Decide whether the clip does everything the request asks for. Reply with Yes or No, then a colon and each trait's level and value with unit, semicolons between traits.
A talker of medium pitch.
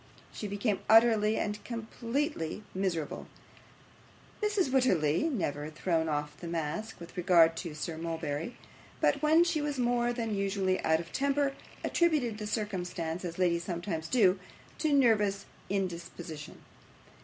No: high, 195 Hz